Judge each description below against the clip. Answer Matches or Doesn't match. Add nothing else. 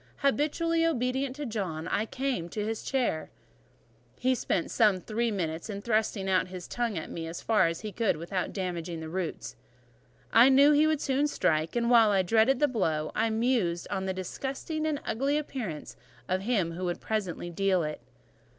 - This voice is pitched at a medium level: Doesn't match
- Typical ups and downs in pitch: Doesn't match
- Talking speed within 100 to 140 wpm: Doesn't match